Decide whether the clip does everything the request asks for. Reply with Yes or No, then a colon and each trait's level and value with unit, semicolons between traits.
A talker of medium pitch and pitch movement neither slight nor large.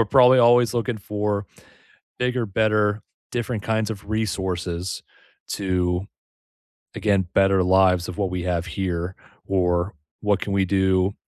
No: low, 100 Hz; average, 3.0 semitones